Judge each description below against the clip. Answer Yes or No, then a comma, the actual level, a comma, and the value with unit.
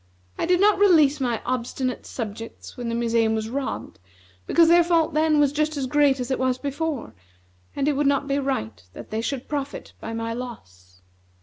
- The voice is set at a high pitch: Yes, very high, 270 Hz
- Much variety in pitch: No, average, 4.4 semitones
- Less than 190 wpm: No, average, 195 wpm